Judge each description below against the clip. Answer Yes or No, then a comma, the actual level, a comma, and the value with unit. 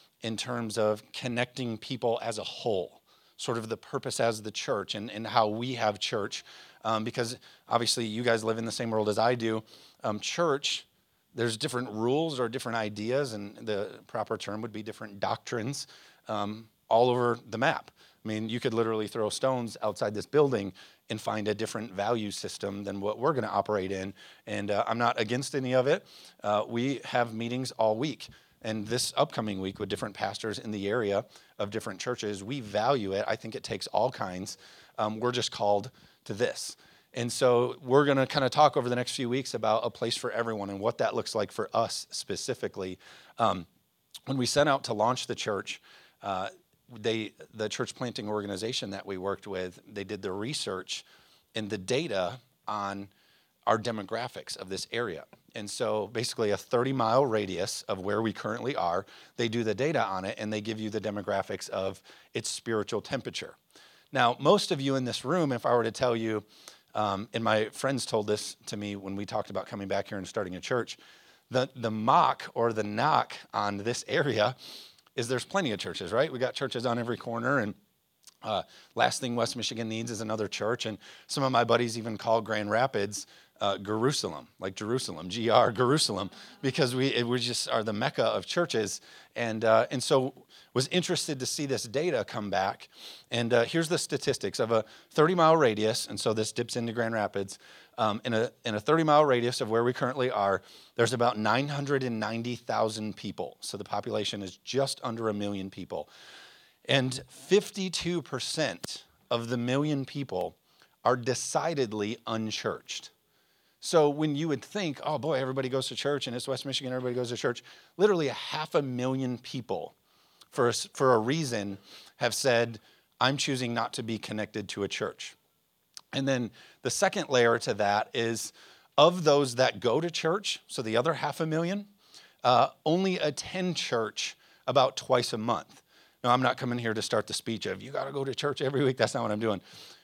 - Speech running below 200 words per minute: Yes, average, 190 wpm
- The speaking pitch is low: Yes, low, 115 Hz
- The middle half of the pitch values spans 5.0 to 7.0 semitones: No, average, 3.5 semitones